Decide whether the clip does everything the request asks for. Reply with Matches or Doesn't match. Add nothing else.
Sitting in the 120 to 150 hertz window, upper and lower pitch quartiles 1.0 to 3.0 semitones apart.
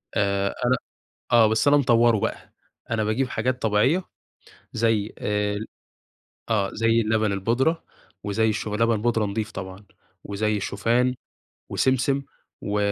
Doesn't match